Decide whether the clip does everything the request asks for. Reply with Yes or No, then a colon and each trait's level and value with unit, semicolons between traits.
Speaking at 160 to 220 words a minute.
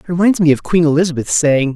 No: fast, 240 wpm